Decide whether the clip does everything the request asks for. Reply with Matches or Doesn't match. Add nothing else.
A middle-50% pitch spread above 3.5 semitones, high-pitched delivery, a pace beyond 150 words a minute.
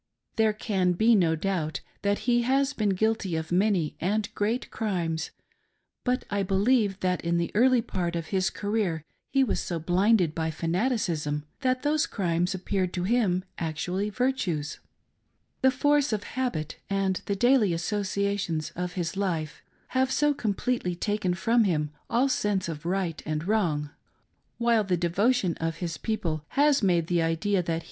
Matches